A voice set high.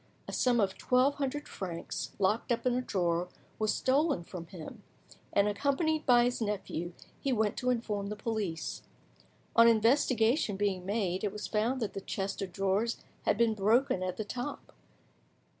Yes: high, 215 Hz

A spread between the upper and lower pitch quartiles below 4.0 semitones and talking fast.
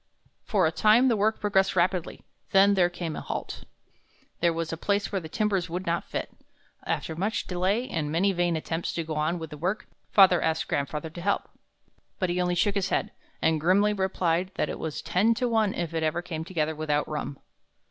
Yes: average, 3.6 semitones; fast, 210 wpm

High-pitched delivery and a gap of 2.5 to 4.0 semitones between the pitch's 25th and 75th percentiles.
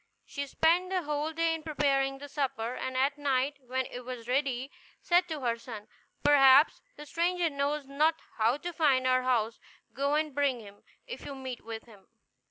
Yes: very high, 275 Hz; average, 2.9 semitones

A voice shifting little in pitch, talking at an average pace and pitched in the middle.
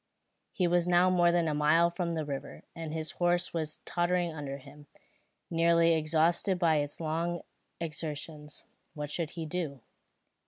Yes: narrow, 2.2 semitones; average, 155 wpm; medium, 165 Hz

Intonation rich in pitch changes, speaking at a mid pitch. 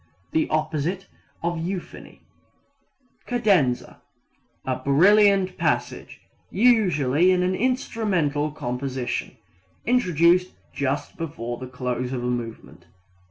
Yes: wide, 6.4 semitones; medium, 155 Hz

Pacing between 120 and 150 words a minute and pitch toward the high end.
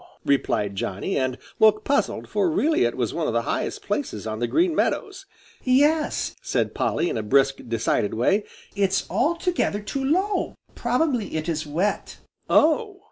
No: average, 160 wpm; high, 215 Hz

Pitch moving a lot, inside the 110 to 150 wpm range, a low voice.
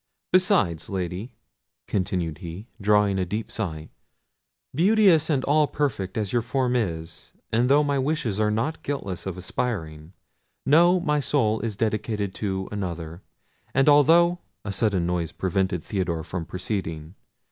Yes: wide, 7.4 semitones; average, 140 wpm; low, 105 Hz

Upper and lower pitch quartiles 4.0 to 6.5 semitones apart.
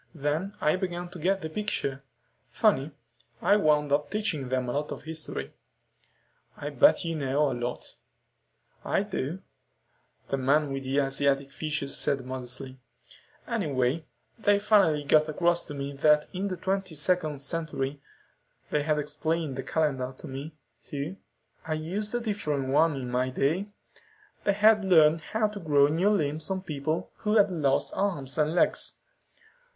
Yes: average, 4.7 semitones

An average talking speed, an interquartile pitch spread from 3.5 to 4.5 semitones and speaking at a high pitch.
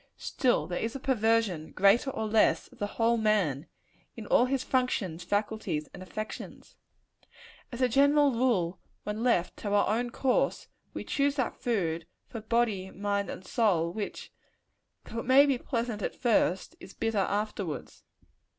Yes: average, 160 wpm; average, 4.0 semitones; high, 220 Hz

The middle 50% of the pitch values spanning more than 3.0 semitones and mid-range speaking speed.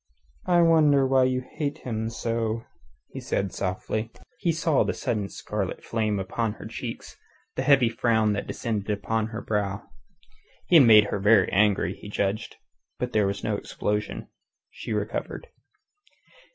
Yes: average, 3.7 semitones; average, 150 wpm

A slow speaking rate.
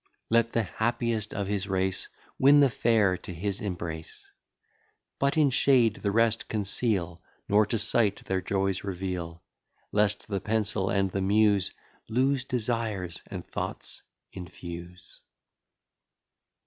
Yes: slow, 125 wpm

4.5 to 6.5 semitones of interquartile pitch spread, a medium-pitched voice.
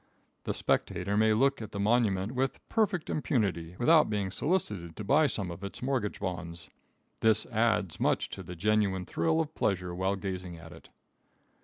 No: average, 5.2 semitones; low, 100 Hz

